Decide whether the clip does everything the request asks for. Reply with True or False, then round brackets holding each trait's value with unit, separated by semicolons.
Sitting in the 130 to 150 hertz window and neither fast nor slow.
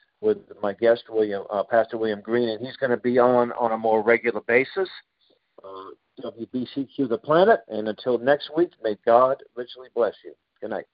False (120 Hz; 185 wpm)